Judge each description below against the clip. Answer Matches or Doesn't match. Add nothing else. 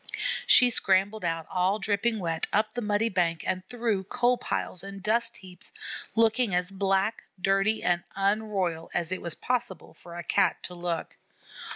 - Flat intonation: Doesn't match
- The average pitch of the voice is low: Doesn't match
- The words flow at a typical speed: Matches